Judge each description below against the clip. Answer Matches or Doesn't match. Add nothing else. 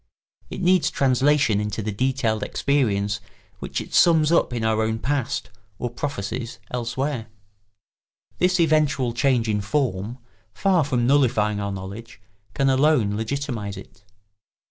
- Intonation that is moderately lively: Matches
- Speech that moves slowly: Matches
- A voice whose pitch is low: Matches